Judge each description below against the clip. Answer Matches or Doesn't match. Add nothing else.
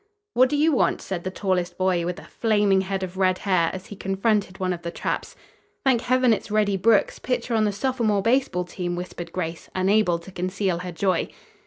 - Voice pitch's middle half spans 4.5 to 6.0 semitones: Doesn't match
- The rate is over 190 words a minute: Matches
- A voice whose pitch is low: Doesn't match